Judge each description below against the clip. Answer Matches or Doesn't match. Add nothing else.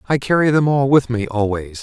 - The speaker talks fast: Matches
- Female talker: Doesn't match